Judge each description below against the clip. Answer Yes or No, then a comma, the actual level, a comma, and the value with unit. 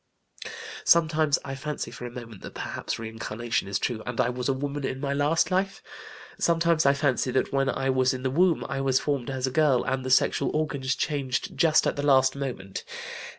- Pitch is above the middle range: No, low, 135 Hz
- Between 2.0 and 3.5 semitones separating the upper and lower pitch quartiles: Yes, narrow, 2.6 semitones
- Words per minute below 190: No, fast, 205 wpm